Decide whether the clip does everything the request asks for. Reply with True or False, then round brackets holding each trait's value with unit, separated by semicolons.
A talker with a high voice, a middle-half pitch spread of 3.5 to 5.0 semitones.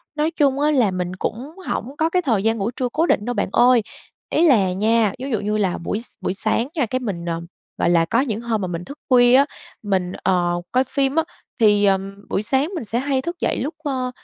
False (230 Hz; 5.5 semitones)